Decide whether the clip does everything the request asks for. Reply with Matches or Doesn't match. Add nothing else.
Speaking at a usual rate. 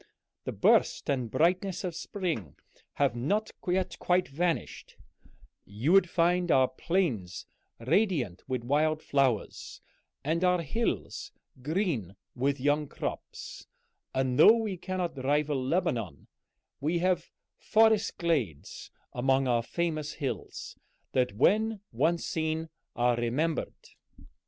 Doesn't match